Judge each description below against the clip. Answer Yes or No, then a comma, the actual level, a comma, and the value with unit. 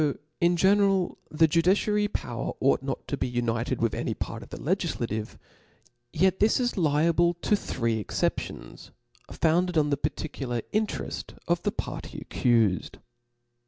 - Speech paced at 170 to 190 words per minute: No, average, 145 wpm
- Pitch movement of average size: No, wide, 7.0 semitones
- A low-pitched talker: No, medium, 155 Hz